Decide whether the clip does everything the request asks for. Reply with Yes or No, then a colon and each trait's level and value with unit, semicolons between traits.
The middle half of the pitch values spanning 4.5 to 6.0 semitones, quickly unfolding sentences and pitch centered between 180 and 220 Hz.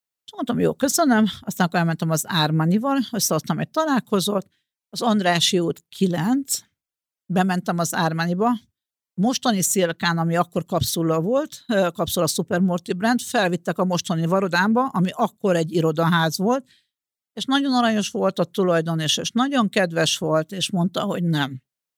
No: average, 5.0 semitones; average, 145 wpm; medium, 185 Hz